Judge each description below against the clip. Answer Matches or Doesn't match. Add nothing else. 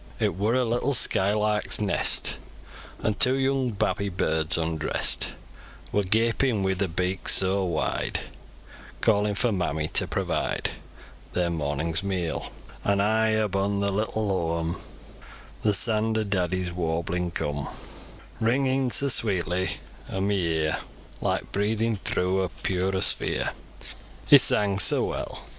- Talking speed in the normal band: Doesn't match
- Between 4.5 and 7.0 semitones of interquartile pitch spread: Doesn't match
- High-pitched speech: Doesn't match